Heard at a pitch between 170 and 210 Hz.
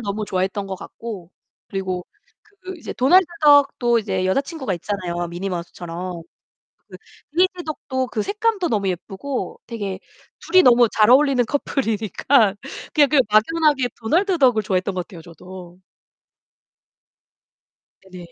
No: high, 220 Hz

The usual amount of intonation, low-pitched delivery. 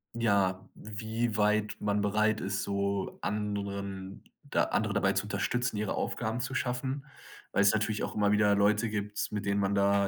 No: narrow, 1.5 semitones; low, 105 Hz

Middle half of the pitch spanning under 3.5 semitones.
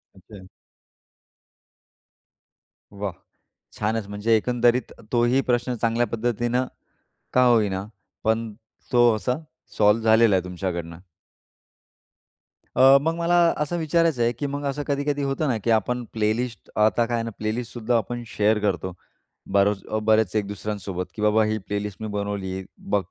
Yes: average, 3.1 semitones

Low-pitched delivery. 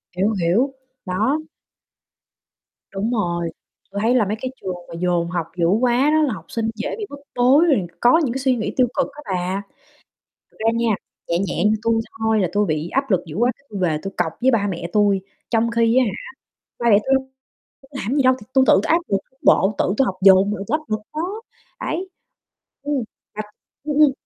No: high, 220 Hz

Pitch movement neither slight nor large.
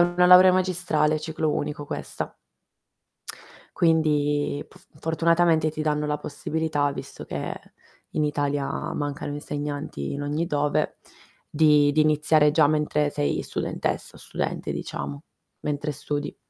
No: narrow, 1.6 semitones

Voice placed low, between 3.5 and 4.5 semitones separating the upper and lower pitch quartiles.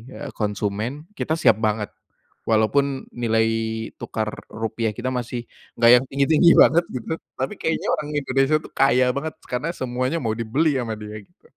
Yes: low, 125 Hz; average, 4.0 semitones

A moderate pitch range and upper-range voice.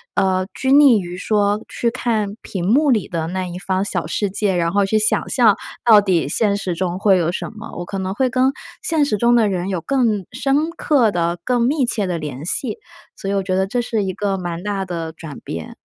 Yes: average, 4.5 semitones; high, 200 Hz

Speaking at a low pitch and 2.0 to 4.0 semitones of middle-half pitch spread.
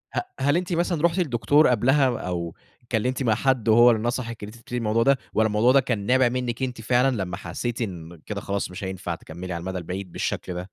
No: low, 115 Hz; average, 5.1 semitones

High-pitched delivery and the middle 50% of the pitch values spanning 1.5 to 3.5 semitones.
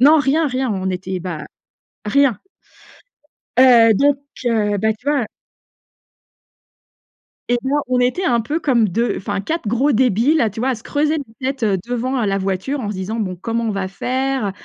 No: high, 235 Hz; average, 4.7 semitones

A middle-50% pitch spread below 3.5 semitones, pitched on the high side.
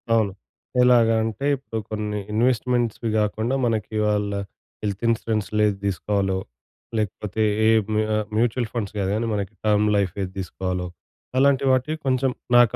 No: average, 2.8 semitones; low, 110 Hz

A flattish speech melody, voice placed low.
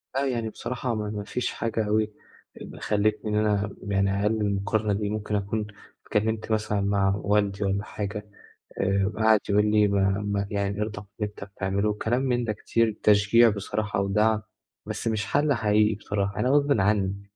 Yes: narrow, 1.4 semitones; low, 105 Hz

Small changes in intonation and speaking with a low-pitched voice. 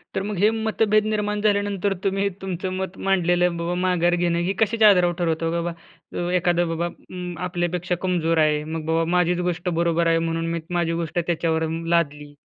No: narrow, 2.3 semitones; medium, 175 Hz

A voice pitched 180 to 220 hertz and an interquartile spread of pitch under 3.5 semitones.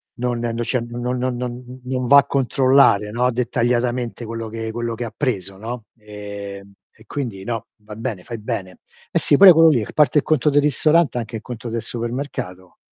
No: low, 120 Hz; average, 2.7 semitones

